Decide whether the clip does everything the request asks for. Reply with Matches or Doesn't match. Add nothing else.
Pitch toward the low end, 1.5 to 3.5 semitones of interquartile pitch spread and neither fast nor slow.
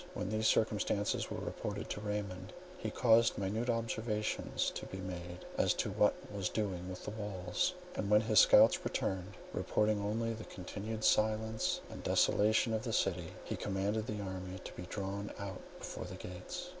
Matches